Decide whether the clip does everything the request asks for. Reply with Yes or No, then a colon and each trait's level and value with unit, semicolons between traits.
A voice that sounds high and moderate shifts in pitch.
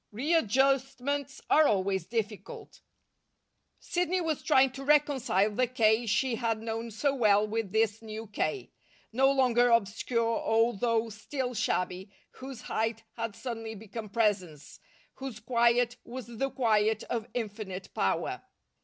Yes: high, 230 Hz; average, 3.3 semitones